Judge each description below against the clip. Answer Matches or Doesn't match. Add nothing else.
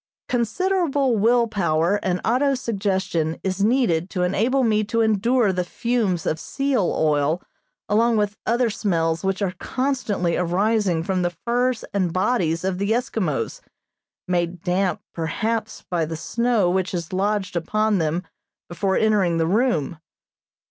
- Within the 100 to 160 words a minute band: Matches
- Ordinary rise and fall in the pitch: Matches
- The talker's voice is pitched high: Matches